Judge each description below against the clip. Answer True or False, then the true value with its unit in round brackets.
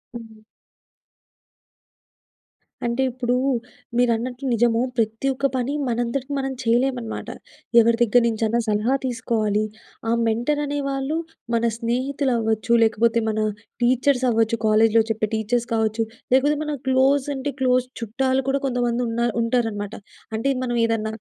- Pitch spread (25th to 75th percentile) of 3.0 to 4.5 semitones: False (2.6 semitones)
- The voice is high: True (235 Hz)